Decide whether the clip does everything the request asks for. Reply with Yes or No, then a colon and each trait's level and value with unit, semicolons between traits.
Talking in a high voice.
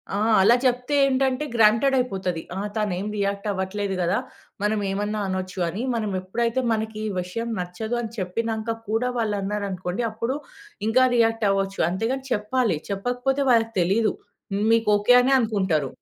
Yes: high, 215 Hz